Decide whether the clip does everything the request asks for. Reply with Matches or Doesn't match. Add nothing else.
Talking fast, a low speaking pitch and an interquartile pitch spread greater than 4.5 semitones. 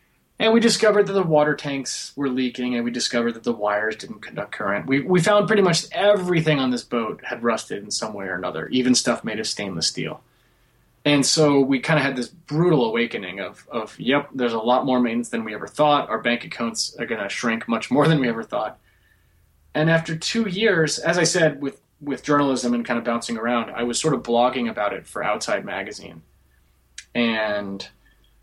Matches